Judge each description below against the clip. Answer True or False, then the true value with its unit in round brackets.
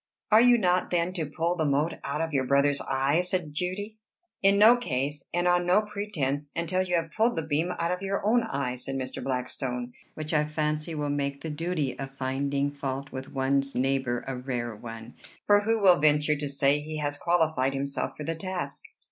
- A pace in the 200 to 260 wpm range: True (205 wpm)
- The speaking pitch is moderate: True (150 Hz)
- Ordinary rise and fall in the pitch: True (4.5 semitones)